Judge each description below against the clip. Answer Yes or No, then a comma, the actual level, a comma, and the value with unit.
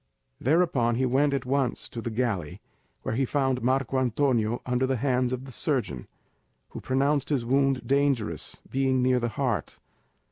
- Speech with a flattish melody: Yes, narrow, 2.3 semitones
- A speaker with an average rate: Yes, average, 165 wpm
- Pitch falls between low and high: No, low, 130 Hz